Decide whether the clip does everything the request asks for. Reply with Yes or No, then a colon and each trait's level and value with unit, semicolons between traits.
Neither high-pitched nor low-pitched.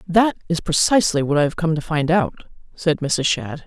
Yes: medium, 165 Hz